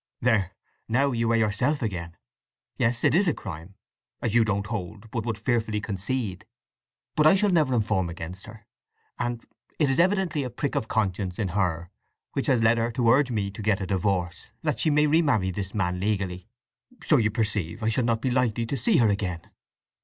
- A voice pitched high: No, low, 110 Hz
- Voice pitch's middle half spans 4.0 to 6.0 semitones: Yes, average, 4.4 semitones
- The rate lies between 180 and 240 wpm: Yes, average, 190 wpm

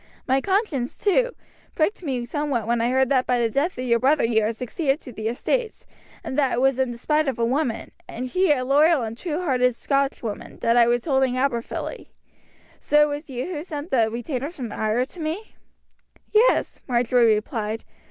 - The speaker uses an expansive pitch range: No, average, 4.1 semitones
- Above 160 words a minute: Yes, average, 190 wpm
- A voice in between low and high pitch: No, very high, 260 Hz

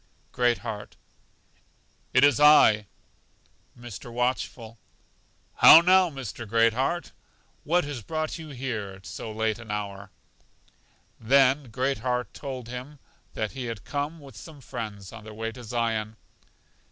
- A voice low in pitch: Yes, low, 120 Hz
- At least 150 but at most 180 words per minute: No, average, 140 wpm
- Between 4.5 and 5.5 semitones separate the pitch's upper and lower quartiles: No, average, 4.1 semitones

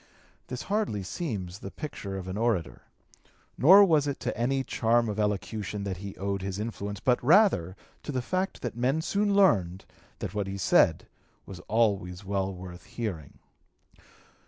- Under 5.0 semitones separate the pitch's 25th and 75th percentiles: No, wide, 5.5 semitones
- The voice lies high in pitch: No, low, 105 Hz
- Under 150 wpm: No, average, 160 wpm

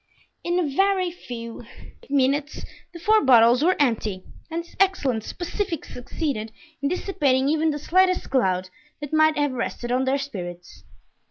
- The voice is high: Yes, very high, 280 Hz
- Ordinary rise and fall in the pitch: No, wide, 5.9 semitones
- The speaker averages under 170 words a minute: Yes, average, 150 wpm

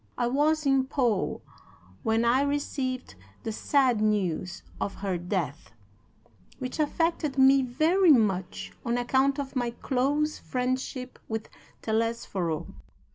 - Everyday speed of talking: No, slow, 120 wpm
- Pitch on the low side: No, very high, 255 Hz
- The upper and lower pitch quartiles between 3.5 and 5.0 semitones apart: Yes, average, 4.1 semitones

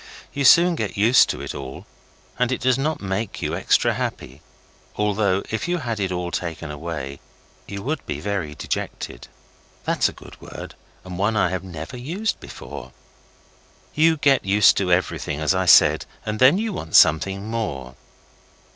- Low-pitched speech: Yes, low, 100 Hz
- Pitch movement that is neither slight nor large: No, wide, 6.6 semitones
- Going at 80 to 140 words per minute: No, average, 175 wpm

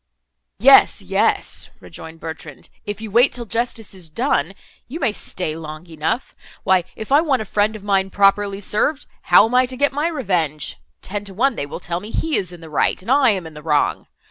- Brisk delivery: Yes, fast, 215 wpm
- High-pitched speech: Yes, high, 200 Hz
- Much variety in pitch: Yes, wide, 6.7 semitones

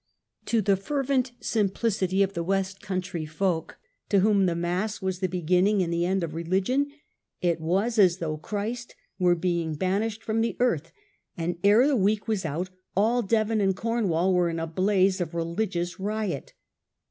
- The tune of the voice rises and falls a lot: No, average, 3.7 semitones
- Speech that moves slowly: No, average, 170 wpm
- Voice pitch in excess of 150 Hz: Yes, high, 190 Hz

